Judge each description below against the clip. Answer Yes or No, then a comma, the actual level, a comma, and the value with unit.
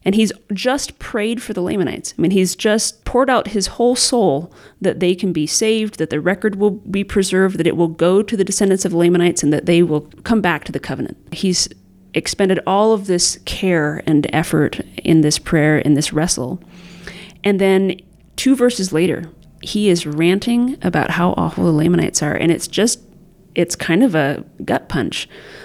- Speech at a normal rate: Yes, average, 190 wpm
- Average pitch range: Yes, average, 3.7 semitones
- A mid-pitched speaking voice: Yes, medium, 180 Hz